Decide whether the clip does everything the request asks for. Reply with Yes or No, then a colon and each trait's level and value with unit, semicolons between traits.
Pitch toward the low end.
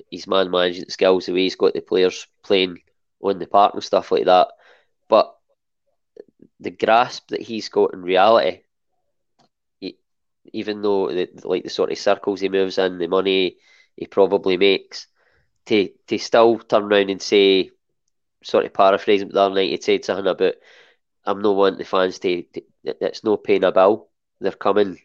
Yes: low, 110 Hz